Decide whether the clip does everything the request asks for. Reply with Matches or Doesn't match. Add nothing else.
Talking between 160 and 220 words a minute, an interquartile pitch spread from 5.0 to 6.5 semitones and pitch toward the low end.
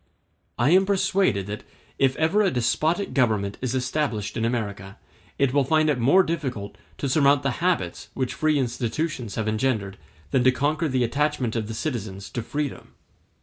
Matches